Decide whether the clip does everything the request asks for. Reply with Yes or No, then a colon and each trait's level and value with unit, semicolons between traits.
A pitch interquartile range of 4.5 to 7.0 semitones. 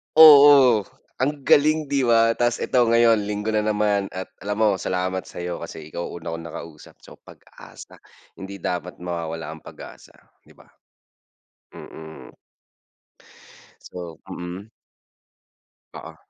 Yes: average, 5.1 semitones